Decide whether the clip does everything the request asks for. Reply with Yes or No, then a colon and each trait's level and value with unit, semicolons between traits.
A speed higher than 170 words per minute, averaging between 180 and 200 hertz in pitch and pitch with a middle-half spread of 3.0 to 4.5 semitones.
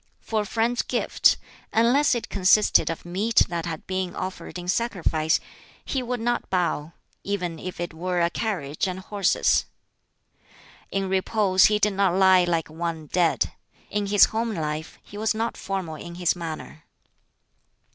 No: average, 155 wpm; medium, 185 Hz; average, 3.7 semitones